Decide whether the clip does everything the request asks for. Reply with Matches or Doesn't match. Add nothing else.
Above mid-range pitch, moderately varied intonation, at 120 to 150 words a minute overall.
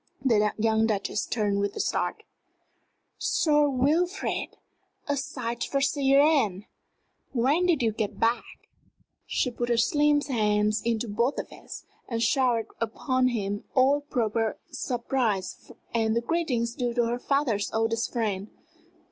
Matches